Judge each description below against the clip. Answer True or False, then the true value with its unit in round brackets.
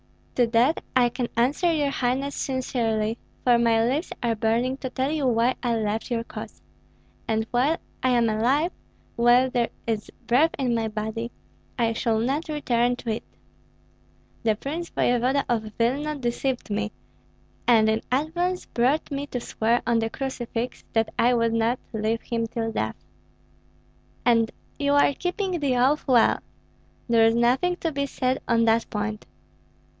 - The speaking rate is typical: True (160 wpm)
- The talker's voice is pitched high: True (240 Hz)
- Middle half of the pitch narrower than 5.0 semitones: True (3.0 semitones)